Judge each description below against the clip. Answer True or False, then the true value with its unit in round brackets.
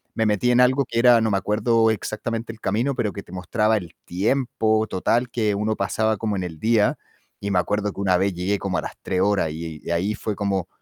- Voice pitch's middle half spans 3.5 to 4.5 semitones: False (2.9 semitones)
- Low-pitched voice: True (105 Hz)